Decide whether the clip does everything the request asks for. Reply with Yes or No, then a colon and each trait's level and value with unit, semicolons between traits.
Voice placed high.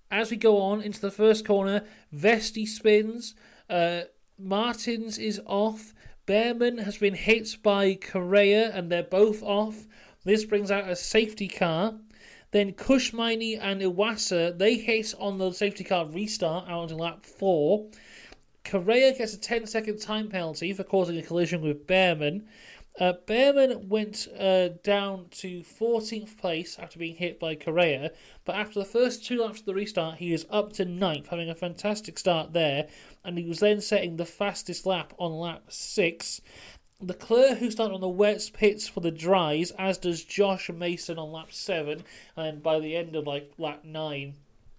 Yes: high, 195 Hz